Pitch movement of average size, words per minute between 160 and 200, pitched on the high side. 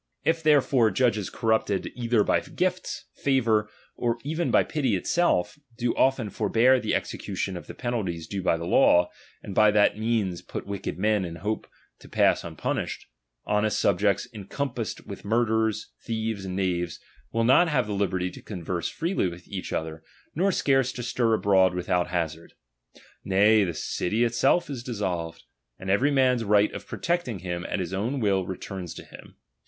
No: average, 4.7 semitones; average, 170 wpm; low, 105 Hz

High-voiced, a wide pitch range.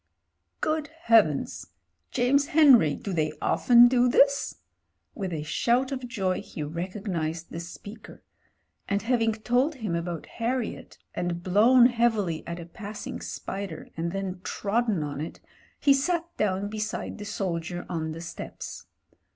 Yes: high, 205 Hz; wide, 6.1 semitones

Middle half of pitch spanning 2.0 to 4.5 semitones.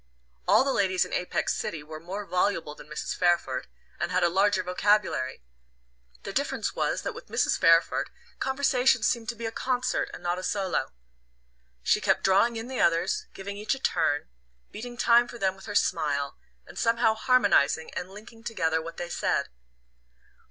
No: wide, 5.4 semitones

